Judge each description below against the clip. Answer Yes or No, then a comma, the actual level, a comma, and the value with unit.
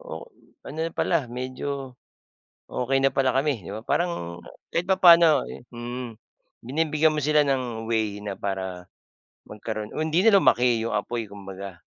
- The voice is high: No, low, 125 Hz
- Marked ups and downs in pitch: Yes, wide, 6.3 semitones